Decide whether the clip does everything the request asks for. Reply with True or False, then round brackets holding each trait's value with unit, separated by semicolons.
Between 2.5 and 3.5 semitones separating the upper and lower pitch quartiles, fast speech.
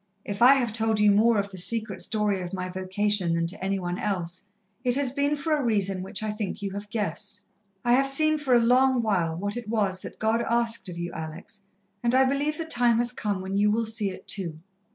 False (4.0 semitones; 235 wpm)